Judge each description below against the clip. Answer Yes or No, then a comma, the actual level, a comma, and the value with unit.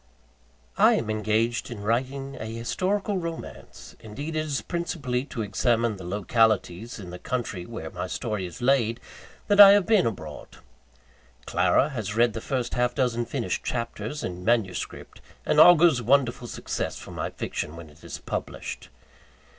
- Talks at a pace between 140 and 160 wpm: Yes, average, 155 wpm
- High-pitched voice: No, low, 120 Hz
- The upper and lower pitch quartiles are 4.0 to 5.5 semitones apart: Yes, average, 4.5 semitones